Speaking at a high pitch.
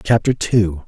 No: low, 105 Hz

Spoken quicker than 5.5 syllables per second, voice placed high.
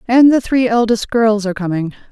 Yes: 5.7 syllables/s; high, 225 Hz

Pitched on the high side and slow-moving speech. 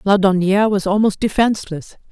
Yes: high, 200 Hz; slow, 115 wpm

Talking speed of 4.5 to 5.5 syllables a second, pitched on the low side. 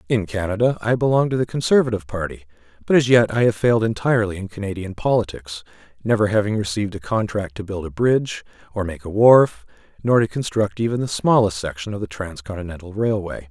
No: 6.2 syllables/s; low, 105 Hz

